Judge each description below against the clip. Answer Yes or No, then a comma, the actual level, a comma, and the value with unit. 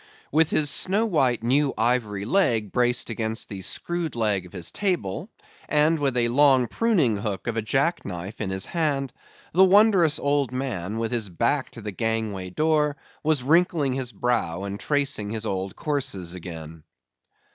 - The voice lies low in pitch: Yes, low, 125 Hz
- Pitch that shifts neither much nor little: No, wide, 6.4 semitones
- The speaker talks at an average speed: Yes, average, 170 wpm